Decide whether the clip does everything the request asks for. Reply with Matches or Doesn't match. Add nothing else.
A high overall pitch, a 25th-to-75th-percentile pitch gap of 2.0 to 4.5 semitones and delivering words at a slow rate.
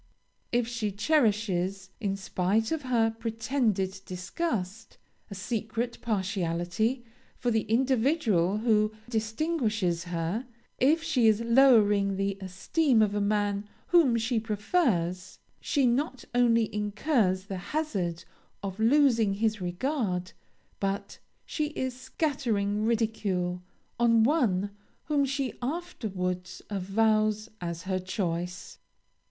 Matches